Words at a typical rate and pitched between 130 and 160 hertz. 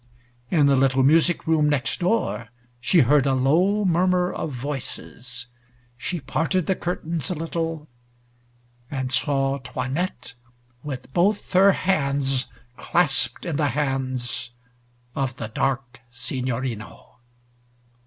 No: slow, 115 wpm; medium, 140 Hz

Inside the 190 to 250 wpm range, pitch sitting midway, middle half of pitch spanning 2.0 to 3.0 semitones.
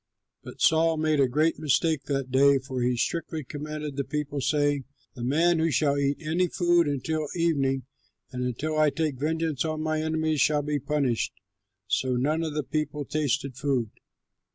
No: average, 175 wpm; medium, 150 Hz; narrow, 2.6 semitones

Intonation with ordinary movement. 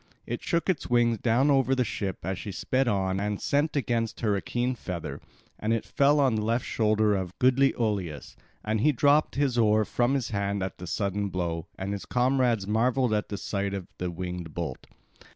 Yes: average, 4.4 semitones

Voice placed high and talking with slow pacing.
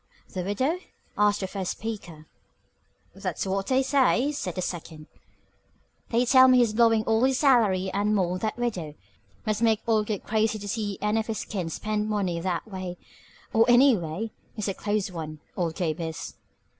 No: high, 210 Hz; average, 180 wpm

